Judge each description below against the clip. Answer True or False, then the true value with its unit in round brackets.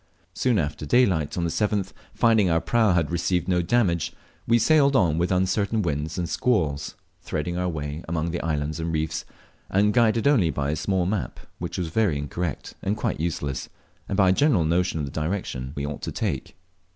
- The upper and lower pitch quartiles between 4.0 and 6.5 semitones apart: True (4.7 semitones)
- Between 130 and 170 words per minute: False (190 wpm)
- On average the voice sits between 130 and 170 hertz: False (85 Hz)